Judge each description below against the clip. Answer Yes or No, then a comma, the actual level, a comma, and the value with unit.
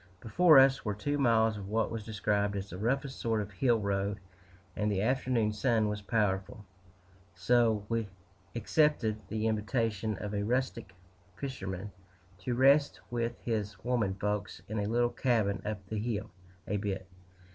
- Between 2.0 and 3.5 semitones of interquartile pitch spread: Yes, average, 2.8 semitones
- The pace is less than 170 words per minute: Yes, average, 155 wpm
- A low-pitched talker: Yes, low, 110 Hz